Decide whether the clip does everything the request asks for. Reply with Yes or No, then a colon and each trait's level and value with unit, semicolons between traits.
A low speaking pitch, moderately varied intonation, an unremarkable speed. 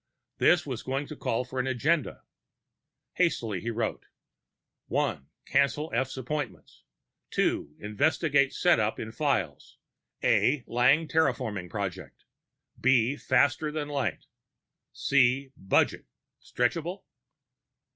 No: low, 130 Hz; average, 4.5 semitones; slow, 105 wpm